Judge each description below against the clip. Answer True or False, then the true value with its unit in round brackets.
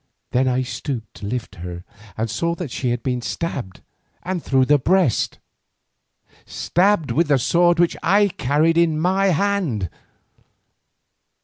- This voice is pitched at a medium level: True (145 Hz)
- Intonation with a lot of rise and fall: True (6.0 semitones)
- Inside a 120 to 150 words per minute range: True (140 wpm)